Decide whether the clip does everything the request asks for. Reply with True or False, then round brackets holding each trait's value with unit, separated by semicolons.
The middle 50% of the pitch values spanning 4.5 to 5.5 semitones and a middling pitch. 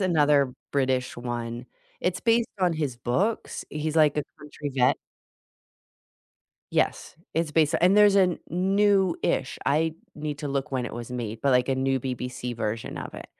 True (5.1 semitones; 145 Hz)